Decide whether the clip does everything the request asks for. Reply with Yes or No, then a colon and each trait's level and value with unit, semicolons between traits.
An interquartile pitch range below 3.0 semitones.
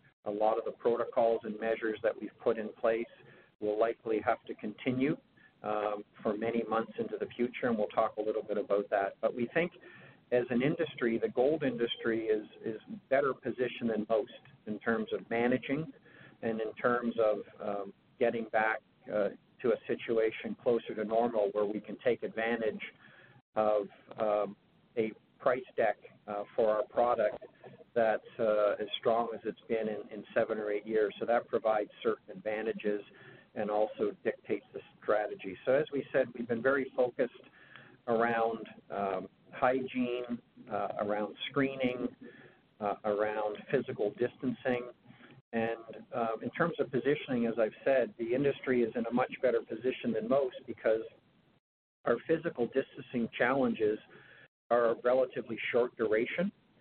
Yes: narrow, 2.5 semitones